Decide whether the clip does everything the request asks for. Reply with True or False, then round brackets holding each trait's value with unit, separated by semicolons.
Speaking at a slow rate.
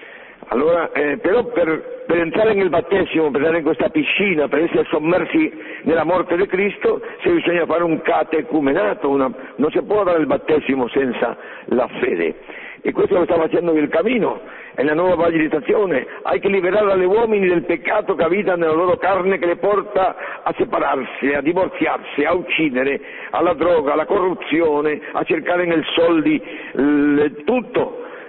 False (165 wpm)